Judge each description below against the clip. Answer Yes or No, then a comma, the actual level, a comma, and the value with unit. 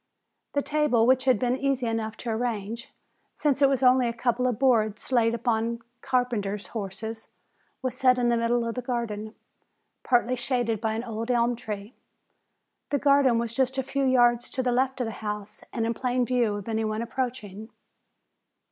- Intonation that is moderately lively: No, narrow, 2.3 semitones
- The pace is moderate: Yes, average, 185 wpm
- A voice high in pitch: Yes, high, 240 Hz